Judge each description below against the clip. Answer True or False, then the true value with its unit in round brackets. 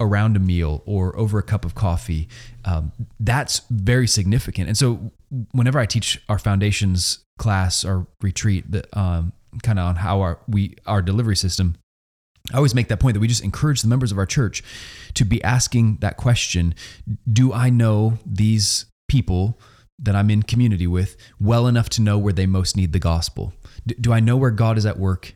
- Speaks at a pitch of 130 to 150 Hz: False (105 Hz)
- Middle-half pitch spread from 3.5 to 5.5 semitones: True (3.8 semitones)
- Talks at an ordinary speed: True (190 wpm)